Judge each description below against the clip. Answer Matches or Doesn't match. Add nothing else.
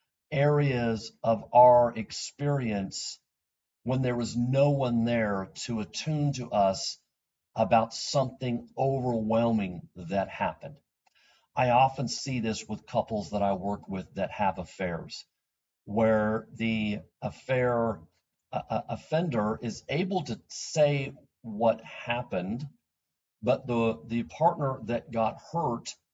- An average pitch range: Matches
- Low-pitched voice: Matches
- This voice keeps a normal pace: Doesn't match